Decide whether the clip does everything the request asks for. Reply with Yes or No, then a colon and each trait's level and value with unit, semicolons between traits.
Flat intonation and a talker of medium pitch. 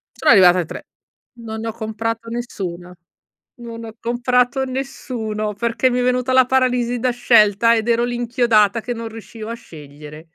No: narrow, 2.3 semitones; high, 230 Hz